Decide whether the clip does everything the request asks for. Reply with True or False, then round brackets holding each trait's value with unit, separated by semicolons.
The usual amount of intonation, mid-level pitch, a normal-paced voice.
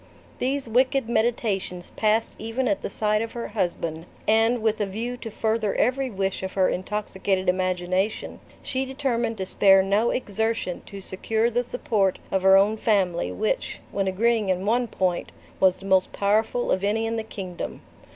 False (3.3 semitones; 210 Hz; 170 wpm)